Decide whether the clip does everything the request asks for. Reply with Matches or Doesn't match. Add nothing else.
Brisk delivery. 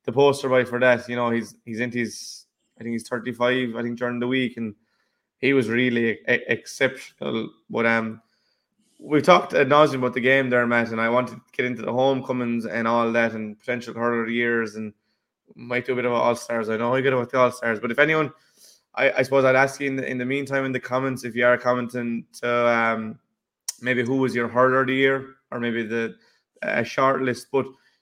Matches